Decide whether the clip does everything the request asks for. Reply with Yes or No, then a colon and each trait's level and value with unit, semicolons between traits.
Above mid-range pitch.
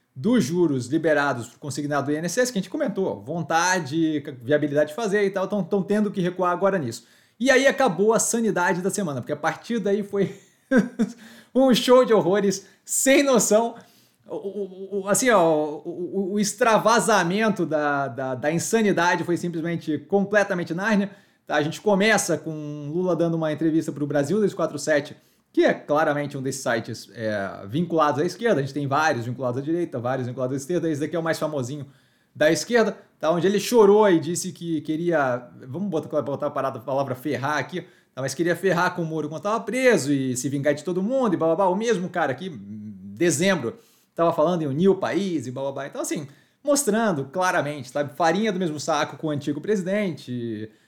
No: medium, 170 Hz